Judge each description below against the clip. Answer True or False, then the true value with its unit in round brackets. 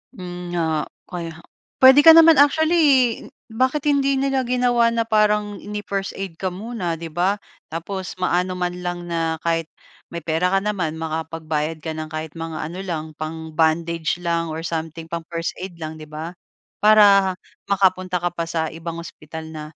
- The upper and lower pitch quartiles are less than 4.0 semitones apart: False (4.3 semitones)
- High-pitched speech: False (175 Hz)